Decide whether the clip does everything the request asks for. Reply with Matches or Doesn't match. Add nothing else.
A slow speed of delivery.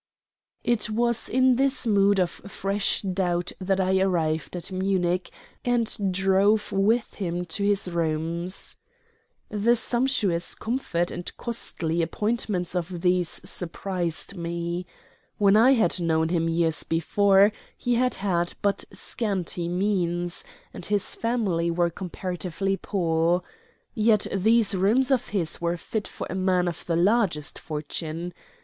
Matches